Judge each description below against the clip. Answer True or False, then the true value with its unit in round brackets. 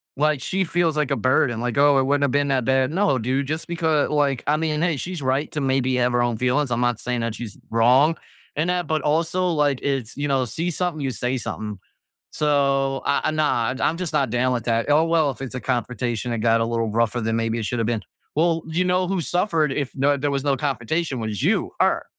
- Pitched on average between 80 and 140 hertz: True (135 Hz)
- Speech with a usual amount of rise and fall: True (4.1 semitones)